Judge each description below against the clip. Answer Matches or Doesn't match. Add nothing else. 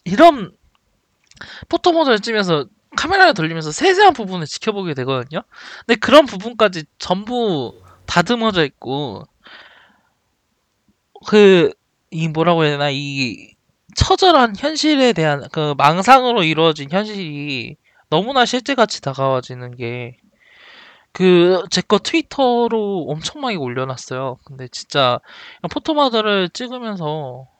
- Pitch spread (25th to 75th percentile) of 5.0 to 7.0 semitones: Doesn't match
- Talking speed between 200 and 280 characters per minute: Matches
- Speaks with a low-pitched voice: Doesn't match